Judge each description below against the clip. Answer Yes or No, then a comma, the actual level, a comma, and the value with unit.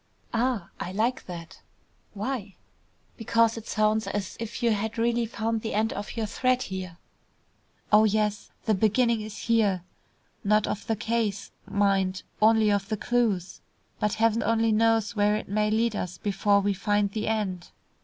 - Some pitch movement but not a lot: No, narrow, 2.0 semitones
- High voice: Yes, high, 215 Hz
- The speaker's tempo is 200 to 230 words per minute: No, average, 165 wpm